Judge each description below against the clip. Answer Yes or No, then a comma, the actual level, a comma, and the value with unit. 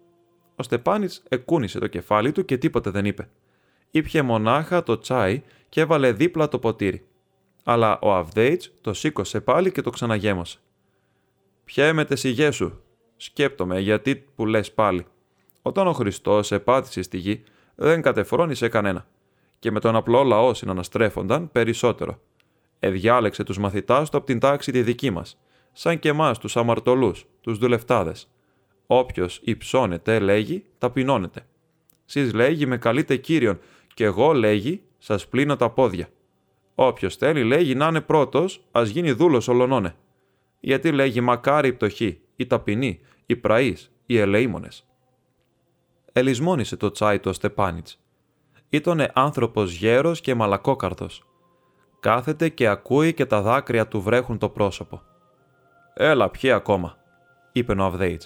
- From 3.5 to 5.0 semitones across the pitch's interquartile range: No, wide, 5.5 semitones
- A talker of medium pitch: No, low, 125 Hz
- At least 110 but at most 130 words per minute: No, average, 140 wpm